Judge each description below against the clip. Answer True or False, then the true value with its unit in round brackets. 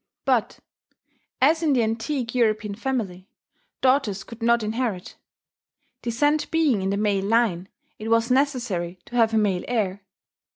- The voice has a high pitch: True (230 Hz)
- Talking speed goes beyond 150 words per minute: False (140 wpm)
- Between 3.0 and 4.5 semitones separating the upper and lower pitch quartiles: True (3.9 semitones)